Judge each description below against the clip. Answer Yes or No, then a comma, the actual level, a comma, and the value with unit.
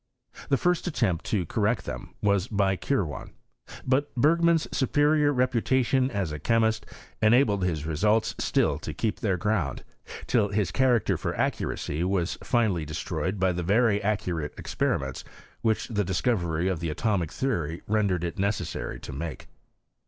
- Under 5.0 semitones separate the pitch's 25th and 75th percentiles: No, wide, 5.6 semitones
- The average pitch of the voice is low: Yes, low, 105 Hz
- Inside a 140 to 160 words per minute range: Yes, average, 150 wpm